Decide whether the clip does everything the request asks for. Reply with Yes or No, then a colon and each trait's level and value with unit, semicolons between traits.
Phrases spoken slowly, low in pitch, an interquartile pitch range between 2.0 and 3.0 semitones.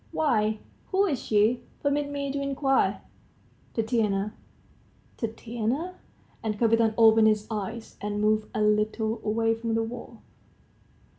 No: slow, 125 wpm; high, 225 Hz; average, 2.7 semitones